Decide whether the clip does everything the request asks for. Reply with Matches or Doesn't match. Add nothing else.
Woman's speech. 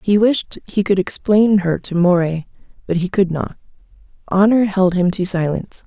Matches